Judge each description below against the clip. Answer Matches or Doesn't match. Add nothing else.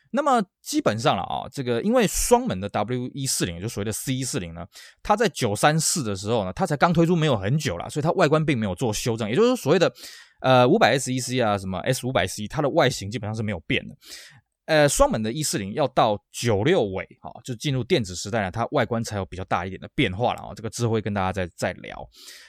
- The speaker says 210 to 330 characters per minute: Doesn't match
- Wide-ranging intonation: Matches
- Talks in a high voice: Doesn't match